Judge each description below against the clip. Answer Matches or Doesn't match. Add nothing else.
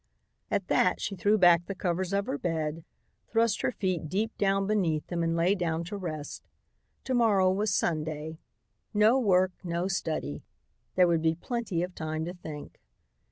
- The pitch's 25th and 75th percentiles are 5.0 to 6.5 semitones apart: Doesn't match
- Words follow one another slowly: Doesn't match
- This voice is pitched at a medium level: Matches